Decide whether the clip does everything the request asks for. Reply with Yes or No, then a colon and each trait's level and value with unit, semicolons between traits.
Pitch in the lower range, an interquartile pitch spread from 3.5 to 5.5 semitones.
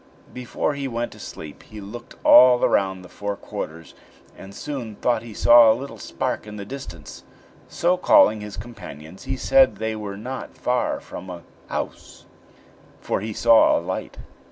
Yes: low, 110 Hz; average, 3.9 semitones